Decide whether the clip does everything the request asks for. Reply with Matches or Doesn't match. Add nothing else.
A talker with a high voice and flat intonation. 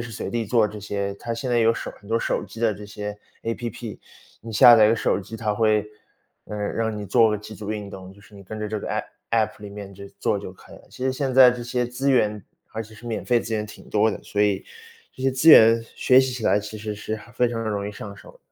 Doesn't match